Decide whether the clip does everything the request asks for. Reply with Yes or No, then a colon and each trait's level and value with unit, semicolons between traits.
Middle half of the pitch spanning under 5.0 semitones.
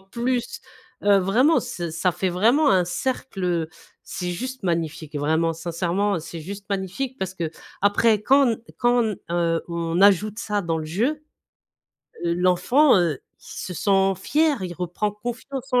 No: wide, 5.6 semitones